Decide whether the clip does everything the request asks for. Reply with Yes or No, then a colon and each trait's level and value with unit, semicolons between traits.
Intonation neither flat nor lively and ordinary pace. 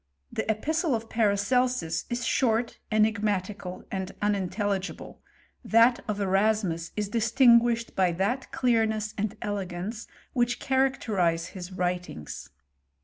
No: average, 3.8 semitones; slow, 110 wpm